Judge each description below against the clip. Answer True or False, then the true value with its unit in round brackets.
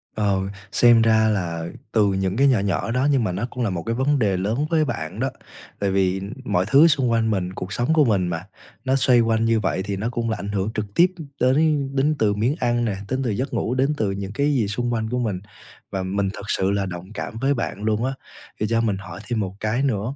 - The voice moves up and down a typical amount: True (4.3 semitones)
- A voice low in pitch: True (110 Hz)